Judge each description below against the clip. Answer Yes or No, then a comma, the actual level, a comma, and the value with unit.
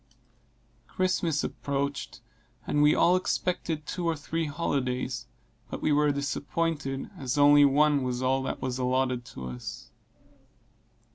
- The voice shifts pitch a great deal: No, average, 2.8 semitones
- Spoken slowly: Yes, slow, 130 wpm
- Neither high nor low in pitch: Yes, medium, 145 Hz